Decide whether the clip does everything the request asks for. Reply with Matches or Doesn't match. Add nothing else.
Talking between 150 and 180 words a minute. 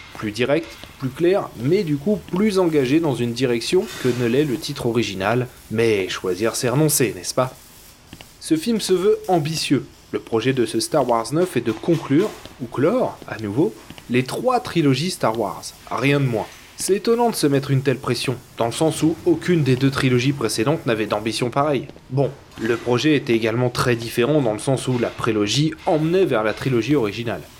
Doesn't match